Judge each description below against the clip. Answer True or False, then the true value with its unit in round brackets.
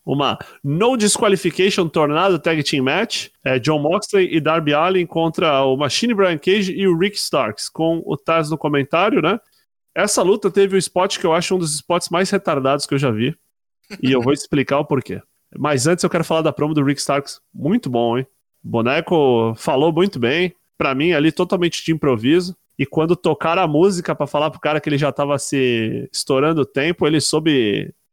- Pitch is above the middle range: False (160 Hz)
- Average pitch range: True (4.3 semitones)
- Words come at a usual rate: False (200 wpm)